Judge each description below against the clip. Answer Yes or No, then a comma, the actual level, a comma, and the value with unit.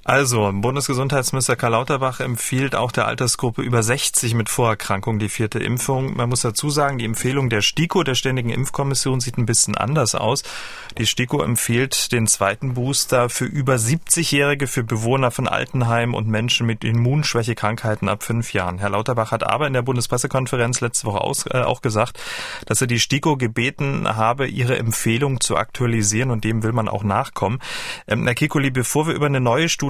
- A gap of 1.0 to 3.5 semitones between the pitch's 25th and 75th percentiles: Yes, average, 2.9 semitones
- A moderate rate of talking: Yes, average, 170 wpm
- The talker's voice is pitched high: No, low, 125 Hz